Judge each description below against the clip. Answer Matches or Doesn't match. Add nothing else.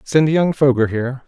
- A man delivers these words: Matches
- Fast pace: Doesn't match